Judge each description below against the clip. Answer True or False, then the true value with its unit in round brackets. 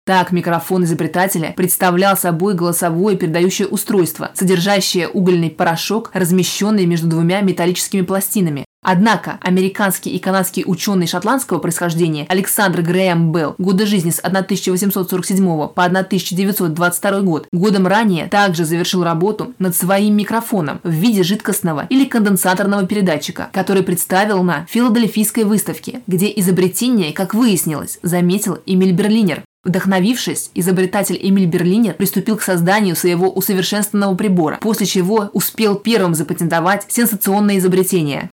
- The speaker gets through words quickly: False (120 wpm)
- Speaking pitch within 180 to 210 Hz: True (190 Hz)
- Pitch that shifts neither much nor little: False (2.3 semitones)